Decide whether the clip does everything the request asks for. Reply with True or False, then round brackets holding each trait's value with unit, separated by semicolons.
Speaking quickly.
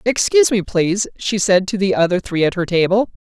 True (220 wpm)